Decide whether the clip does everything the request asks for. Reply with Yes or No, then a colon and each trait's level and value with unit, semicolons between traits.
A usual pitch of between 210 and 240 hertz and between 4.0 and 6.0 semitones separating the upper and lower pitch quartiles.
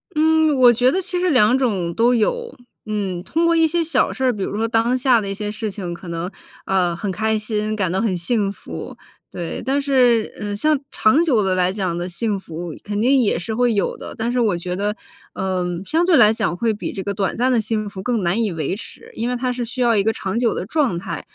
Yes: high, 220 Hz; average, 4.7 semitones